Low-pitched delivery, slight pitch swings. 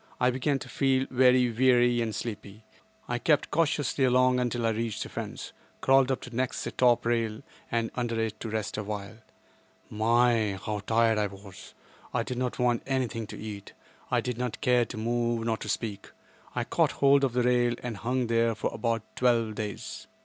Yes: low, 120 Hz; narrow, 2.2 semitones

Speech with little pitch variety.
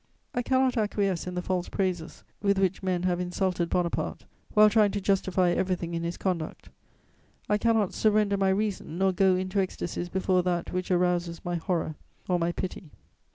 Yes: narrow, 2.1 semitones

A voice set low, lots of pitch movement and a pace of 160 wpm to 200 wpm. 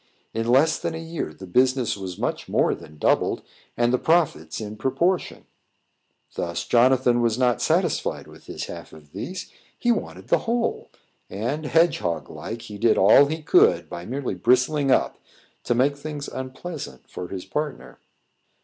Yes: low, 125 Hz; wide, 6.0 semitones; average, 165 wpm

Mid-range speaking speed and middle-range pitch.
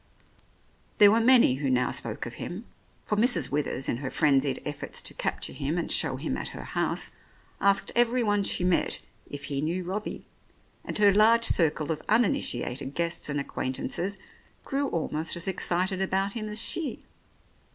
Yes: average, 165 wpm; medium, 175 Hz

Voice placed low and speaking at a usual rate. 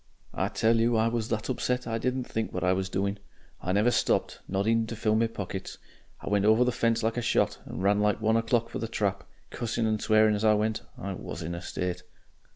No: low, 110 Hz; fast, 240 wpm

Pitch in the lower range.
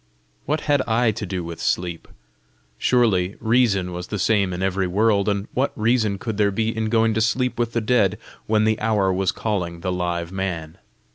Yes: low, 105 Hz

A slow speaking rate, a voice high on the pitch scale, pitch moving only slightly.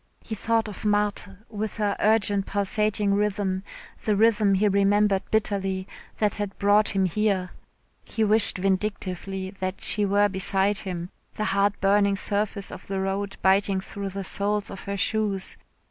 No: average, 155 wpm; high, 200 Hz; narrow, 1.4 semitones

